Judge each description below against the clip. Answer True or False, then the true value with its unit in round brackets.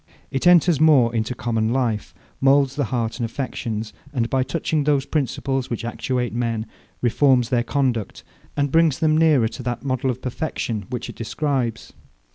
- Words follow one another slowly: False (165 wpm)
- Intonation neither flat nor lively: True (3.4 semitones)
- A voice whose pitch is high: False (130 Hz)